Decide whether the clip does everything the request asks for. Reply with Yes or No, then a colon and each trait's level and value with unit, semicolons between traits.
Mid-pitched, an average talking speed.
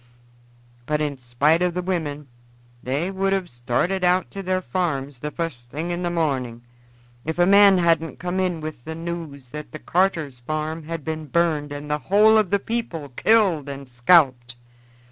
Yes: medium, 160 Hz; average, 175 wpm